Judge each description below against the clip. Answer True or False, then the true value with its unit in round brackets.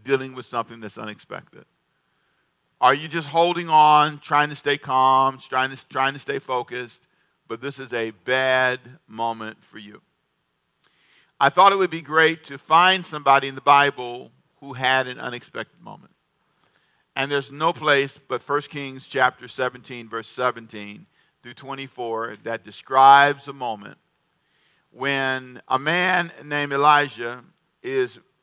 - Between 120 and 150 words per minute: True (145 wpm)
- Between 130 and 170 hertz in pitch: True (135 Hz)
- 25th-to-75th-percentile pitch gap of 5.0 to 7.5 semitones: False (3.1 semitones)